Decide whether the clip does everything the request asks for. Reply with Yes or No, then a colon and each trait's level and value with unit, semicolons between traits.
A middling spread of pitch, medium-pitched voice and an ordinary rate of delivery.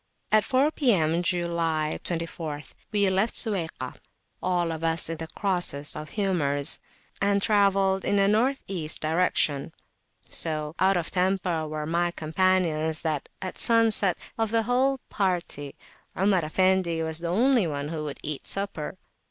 Yes: average, 3.9 semitones; medium, 175 Hz; average, 145 wpm